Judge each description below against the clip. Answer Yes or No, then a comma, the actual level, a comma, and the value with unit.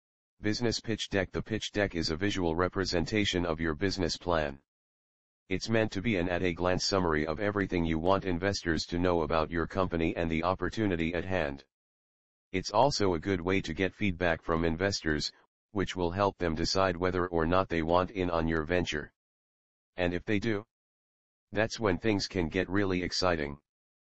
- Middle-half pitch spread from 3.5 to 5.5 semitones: No, average, 2.9 semitones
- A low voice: Yes, very low, 90 Hz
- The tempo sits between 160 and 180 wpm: Yes, average, 175 wpm